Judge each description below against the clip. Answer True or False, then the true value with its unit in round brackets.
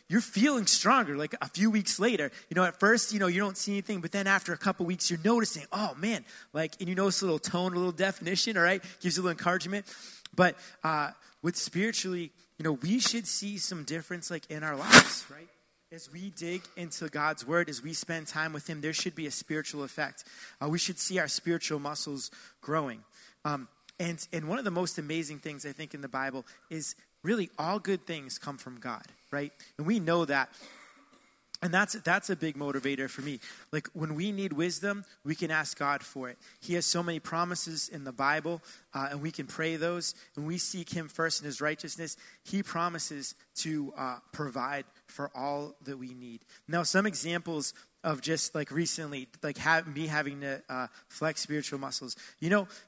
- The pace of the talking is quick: True (210 wpm)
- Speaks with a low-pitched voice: False (165 Hz)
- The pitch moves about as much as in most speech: True (4.0 semitones)